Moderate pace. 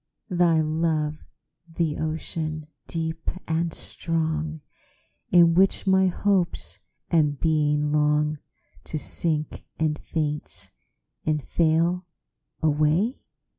No: slow, 85 wpm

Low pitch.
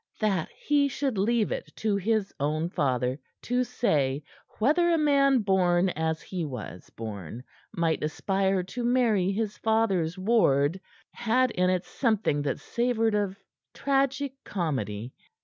No: high, 195 Hz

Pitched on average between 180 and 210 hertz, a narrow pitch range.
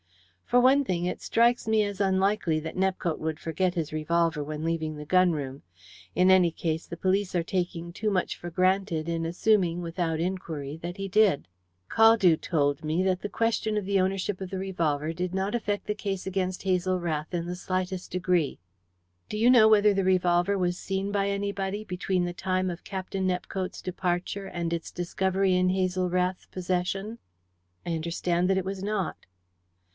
Yes: medium, 185 Hz; narrow, 2.3 semitones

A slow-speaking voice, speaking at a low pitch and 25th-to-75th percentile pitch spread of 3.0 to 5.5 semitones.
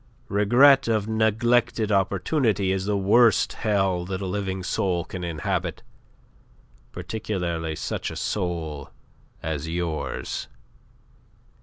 Yes: slow, 105 wpm; very low, 95 Hz; average, 3.9 semitones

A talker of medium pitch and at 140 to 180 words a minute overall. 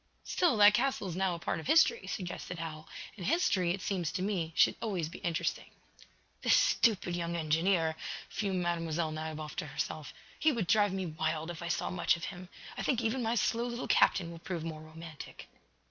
No: medium, 175 Hz; average, 195 wpm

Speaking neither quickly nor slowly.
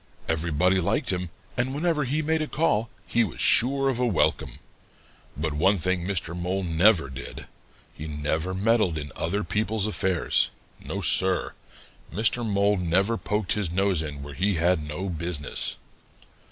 Yes: average, 155 wpm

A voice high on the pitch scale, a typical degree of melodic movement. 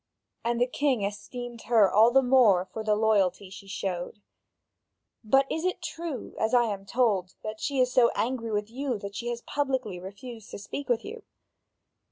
Yes: high, 230 Hz; average, 4.0 semitones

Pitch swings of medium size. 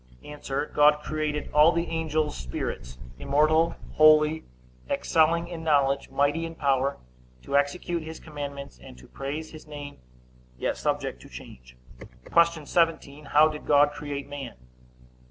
No: narrow, 2.1 semitones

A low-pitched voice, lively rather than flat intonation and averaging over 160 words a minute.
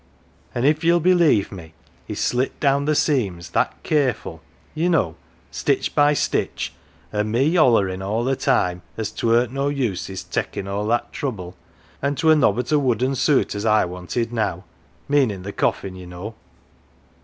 Yes: low, 120 Hz; wide, 6.5 semitones; average, 175 wpm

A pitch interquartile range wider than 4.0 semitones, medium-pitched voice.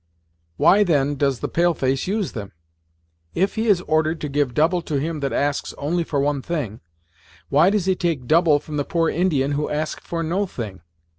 No: average, 3.6 semitones; medium, 155 Hz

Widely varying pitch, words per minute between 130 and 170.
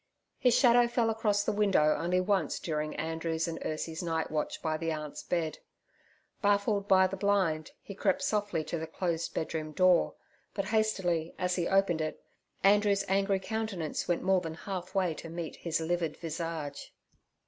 No: average, 3.7 semitones; average, 165 wpm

